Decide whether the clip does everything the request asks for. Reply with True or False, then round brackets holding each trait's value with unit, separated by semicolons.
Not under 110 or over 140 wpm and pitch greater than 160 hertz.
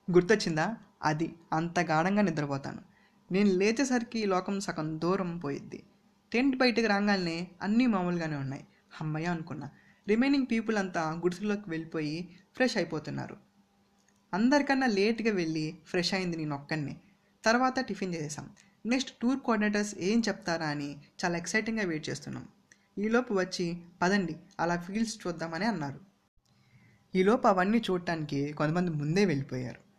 True (120 wpm; 185 Hz)